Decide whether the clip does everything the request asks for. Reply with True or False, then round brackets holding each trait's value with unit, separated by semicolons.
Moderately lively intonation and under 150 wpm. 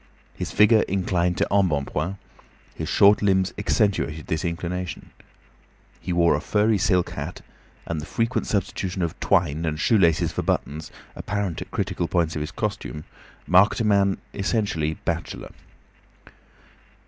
True (3.5 semitones; 140 wpm)